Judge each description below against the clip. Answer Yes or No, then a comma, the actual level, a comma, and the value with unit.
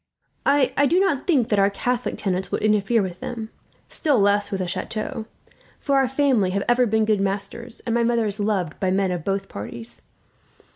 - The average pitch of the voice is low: No, high, 215 Hz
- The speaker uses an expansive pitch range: No, average, 3.9 semitones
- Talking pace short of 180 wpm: No, average, 195 wpm